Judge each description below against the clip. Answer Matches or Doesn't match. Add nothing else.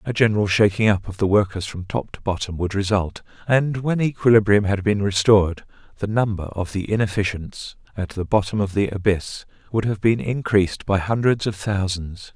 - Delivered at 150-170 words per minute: Doesn't match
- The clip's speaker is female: Doesn't match